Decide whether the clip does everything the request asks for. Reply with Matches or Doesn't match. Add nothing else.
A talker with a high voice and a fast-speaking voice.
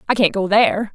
Matches